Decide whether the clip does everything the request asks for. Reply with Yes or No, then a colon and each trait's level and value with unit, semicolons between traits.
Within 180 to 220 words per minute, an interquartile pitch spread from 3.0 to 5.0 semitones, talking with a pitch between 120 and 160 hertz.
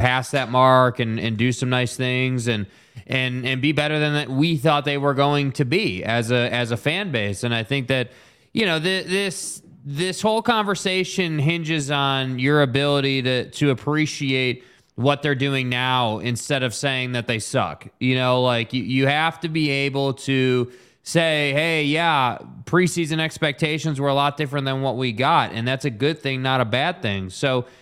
Yes: average, 190 wpm; average, 3.3 semitones; low, 135 Hz